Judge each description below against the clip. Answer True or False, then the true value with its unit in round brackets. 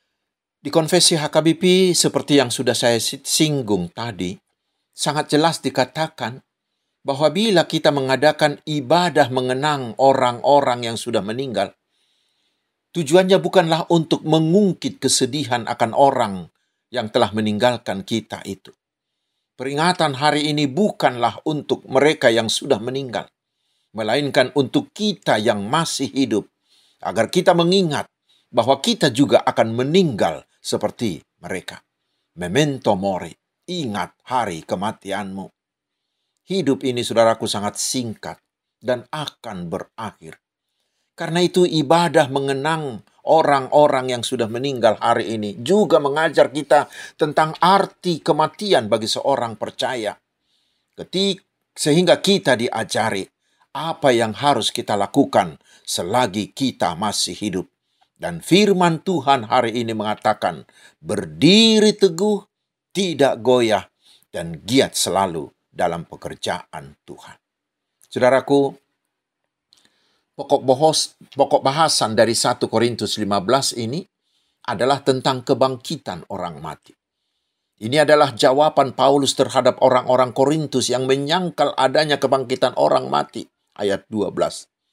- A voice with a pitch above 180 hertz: False (140 Hz)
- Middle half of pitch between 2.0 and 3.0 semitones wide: False (5.0 semitones)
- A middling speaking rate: True (105 wpm)